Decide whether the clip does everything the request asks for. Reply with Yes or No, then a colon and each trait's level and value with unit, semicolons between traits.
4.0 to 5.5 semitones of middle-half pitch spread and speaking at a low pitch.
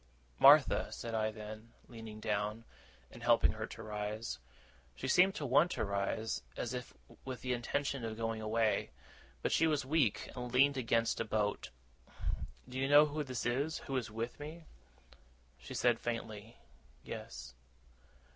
No: average, 3.6 semitones; low, 115 Hz